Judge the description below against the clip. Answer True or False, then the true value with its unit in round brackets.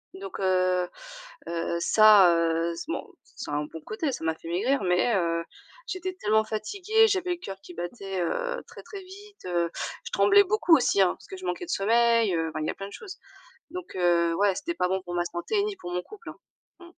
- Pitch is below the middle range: False (205 Hz)